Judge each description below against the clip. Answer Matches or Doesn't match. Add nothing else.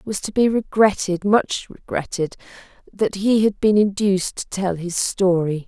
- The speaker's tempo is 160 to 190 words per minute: Doesn't match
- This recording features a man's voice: Doesn't match